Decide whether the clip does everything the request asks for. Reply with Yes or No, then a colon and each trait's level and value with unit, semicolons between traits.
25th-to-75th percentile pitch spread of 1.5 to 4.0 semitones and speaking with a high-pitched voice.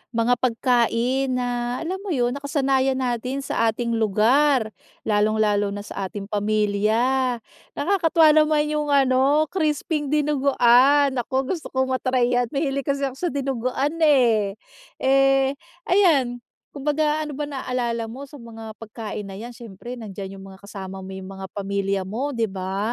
No: average, 4.4 semitones; very high, 250 Hz